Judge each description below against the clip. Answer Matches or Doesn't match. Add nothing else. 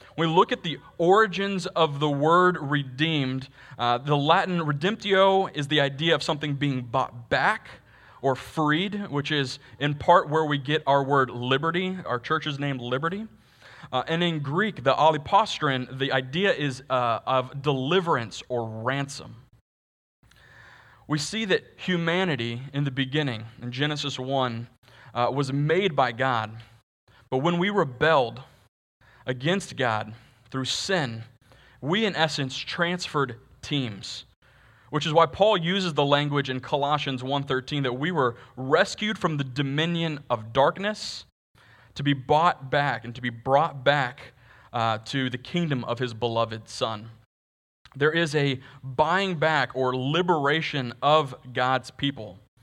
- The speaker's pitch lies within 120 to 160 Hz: Matches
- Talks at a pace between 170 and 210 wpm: Doesn't match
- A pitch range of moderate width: Matches